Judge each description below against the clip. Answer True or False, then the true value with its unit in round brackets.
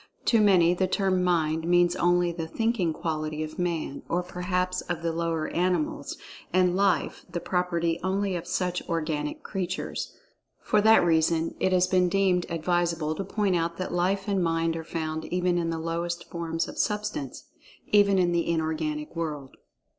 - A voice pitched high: False (175 Hz)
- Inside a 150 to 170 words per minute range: True (165 wpm)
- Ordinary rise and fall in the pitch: False (2.0 semitones)